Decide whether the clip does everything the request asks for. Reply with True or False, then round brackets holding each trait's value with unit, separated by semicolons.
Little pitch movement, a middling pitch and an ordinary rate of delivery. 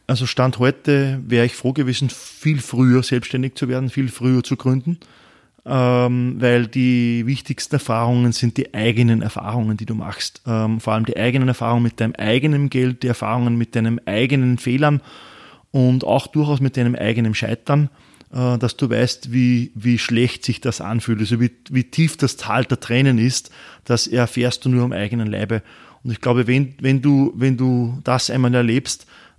False (1.8 semitones; 125 Hz; 175 wpm)